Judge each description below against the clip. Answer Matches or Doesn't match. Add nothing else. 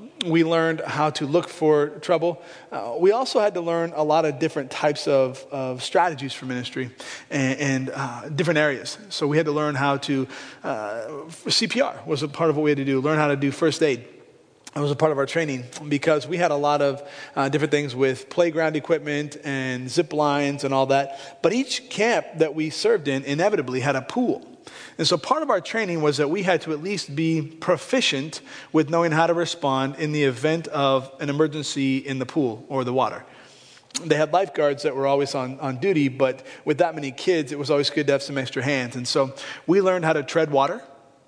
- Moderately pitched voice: Matches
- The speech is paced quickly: Matches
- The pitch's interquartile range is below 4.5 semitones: Matches